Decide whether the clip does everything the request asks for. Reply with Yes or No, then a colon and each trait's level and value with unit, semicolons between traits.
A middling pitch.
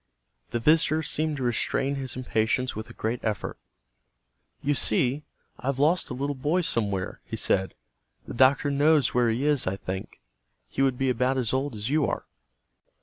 No: low, 130 Hz